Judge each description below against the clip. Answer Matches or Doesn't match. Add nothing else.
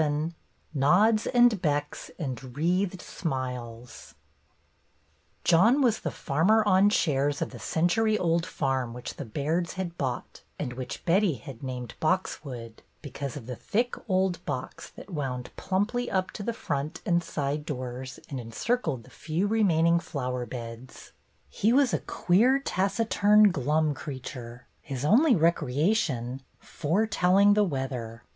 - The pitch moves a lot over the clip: Matches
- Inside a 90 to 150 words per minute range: Matches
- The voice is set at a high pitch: Doesn't match